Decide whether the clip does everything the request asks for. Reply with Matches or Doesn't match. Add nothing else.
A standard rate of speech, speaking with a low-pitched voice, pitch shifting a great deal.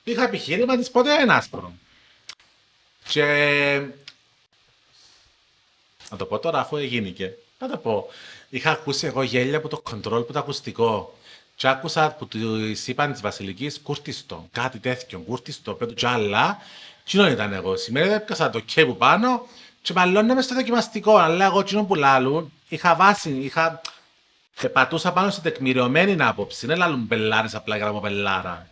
Doesn't match